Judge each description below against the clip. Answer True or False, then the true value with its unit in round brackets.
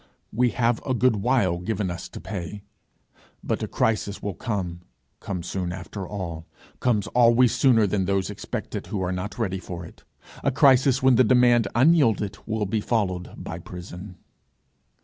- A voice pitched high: False (105 Hz)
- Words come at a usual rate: True (170 wpm)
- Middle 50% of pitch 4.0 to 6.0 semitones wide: True (4.6 semitones)